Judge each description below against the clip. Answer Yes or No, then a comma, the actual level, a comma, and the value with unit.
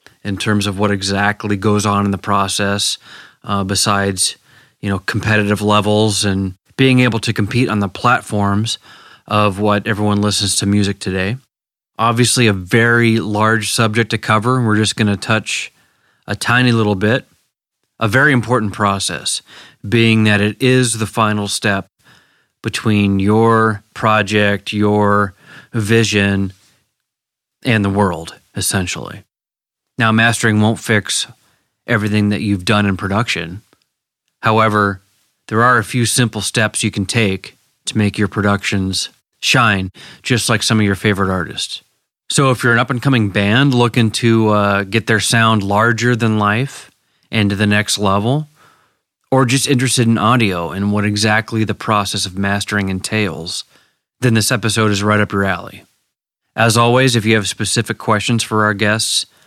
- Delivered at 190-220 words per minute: No, average, 155 wpm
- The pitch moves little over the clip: Yes, narrow, 2.1 semitones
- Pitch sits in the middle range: No, low, 105 Hz